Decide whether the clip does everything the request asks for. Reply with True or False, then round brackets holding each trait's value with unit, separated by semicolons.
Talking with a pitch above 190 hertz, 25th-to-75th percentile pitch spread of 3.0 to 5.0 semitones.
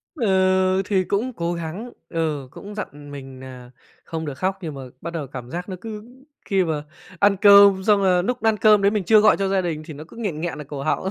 False (185 Hz; 4.7 semitones)